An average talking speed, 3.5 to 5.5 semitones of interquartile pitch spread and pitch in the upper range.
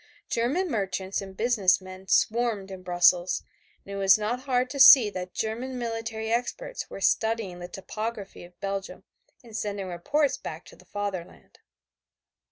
Yes: average, 160 wpm; average, 3.9 semitones; high, 210 Hz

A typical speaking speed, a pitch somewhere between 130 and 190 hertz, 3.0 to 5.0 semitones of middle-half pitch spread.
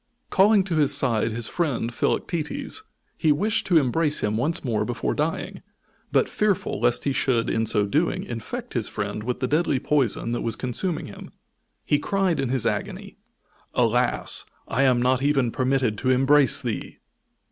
No: average, 170 wpm; low, 135 Hz; wide, 5.4 semitones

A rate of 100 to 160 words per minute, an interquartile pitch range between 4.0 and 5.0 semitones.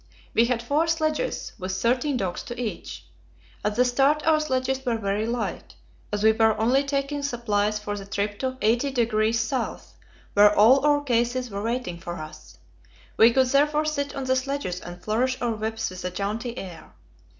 No: average, 180 wpm; average, 4.3 semitones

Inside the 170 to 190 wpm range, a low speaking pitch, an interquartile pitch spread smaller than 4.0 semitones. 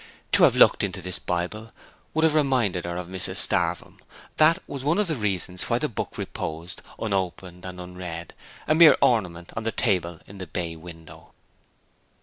No: average, 175 wpm; very low, 90 Hz; average, 4.7 semitones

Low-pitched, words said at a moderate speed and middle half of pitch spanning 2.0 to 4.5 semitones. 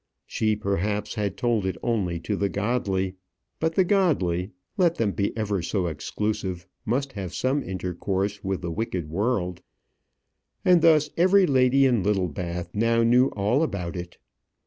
No: low, 105 Hz; average, 150 wpm; average, 5.2 semitones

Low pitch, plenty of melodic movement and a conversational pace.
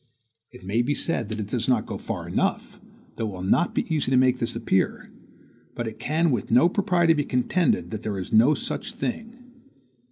No: low, 125 Hz; wide, 5.9 semitones; fast, 210 wpm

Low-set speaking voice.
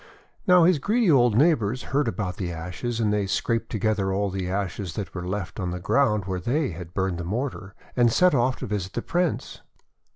Yes: low, 105 Hz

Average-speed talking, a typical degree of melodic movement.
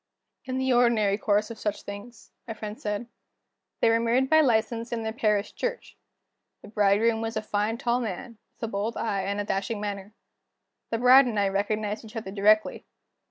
No: average, 190 wpm; narrow, 2.2 semitones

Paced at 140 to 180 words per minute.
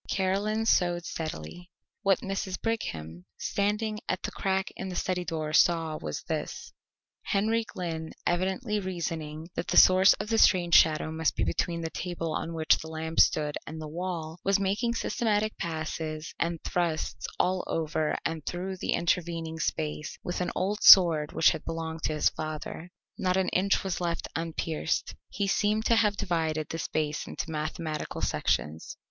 Yes: average, 165 wpm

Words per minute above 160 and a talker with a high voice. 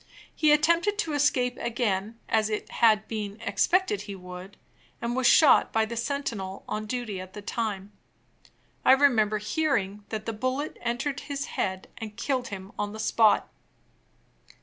No: average, 155 wpm; high, 225 Hz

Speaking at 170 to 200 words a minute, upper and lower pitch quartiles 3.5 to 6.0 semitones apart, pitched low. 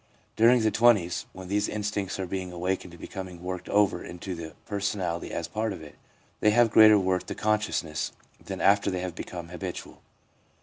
No: average, 180 wpm; average, 3.0 semitones; very low, 95 Hz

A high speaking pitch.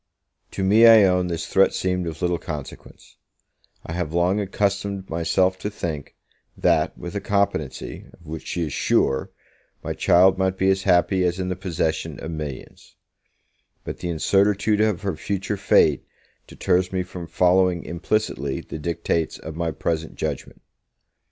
No: very low, 90 Hz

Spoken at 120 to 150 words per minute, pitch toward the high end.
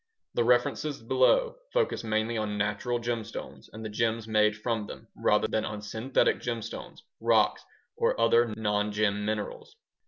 No: average, 145 wpm; low, 110 Hz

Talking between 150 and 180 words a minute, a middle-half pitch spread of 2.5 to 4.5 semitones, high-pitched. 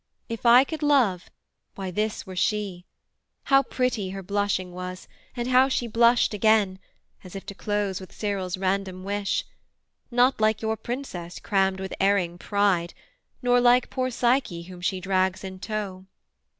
Yes: average, 155 wpm; average, 4.0 semitones; high, 200 Hz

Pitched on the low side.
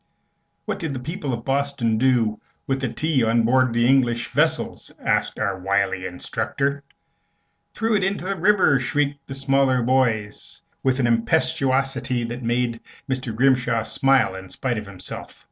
Yes: low, 130 Hz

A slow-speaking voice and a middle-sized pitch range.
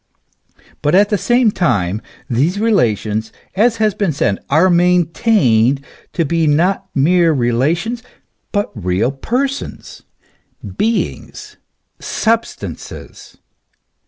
No: slow, 100 wpm; wide, 8.6 semitones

